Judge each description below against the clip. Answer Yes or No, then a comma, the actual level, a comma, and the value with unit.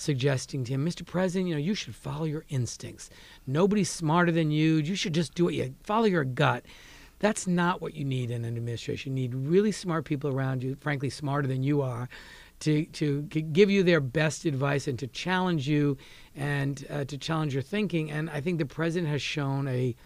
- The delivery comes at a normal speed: No, fast, 210 wpm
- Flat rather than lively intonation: No, average, 3.8 semitones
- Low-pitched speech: No, medium, 150 Hz